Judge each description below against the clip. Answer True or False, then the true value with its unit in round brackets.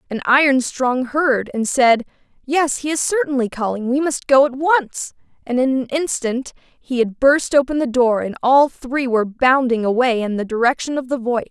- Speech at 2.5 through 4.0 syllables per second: False (4.8 syllables/s)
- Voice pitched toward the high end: True (260 Hz)